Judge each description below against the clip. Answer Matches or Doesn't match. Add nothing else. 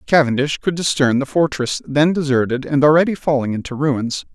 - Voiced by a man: Matches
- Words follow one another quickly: Doesn't match